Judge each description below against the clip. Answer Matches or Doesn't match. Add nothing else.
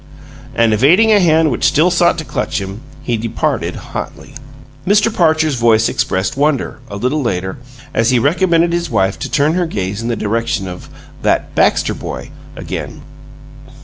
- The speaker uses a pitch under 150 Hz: Matches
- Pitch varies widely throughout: Matches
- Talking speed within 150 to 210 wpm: Matches